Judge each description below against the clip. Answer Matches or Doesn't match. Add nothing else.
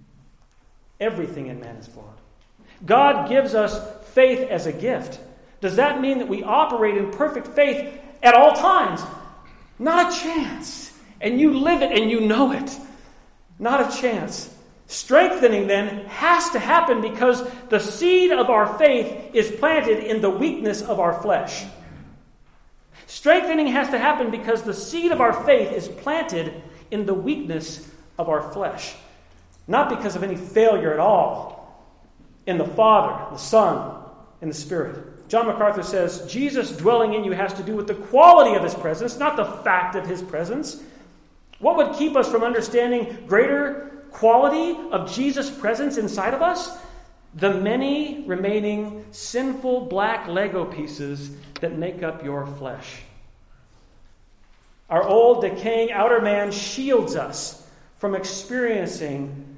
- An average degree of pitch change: Doesn't match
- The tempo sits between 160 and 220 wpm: Doesn't match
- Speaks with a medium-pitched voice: Doesn't match